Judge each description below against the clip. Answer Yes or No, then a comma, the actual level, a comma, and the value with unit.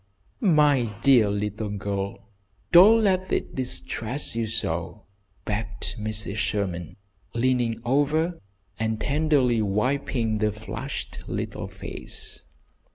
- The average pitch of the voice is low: Yes, low, 115 Hz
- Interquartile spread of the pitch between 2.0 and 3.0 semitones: No, average, 4.8 semitones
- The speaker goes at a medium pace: No, slow, 100 wpm